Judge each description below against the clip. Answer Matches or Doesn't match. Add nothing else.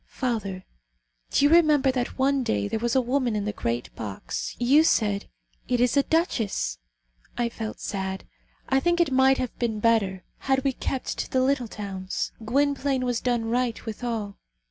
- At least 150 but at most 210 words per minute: Matches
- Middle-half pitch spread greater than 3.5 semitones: Matches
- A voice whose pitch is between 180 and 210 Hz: Doesn't match